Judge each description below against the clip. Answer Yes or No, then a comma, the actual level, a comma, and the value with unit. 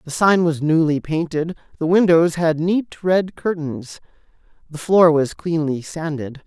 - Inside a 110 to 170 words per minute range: Yes, average, 150 wpm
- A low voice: No, medium, 165 Hz